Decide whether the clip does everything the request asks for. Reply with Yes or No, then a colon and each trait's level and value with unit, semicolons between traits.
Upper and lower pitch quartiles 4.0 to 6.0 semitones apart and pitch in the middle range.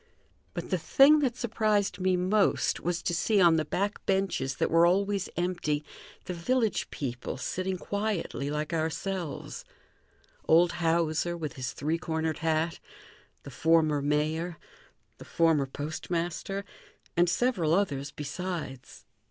No: average, 3.6 semitones; medium, 170 Hz